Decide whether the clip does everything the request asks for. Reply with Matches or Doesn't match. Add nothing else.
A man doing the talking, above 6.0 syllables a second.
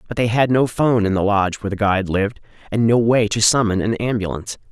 Matches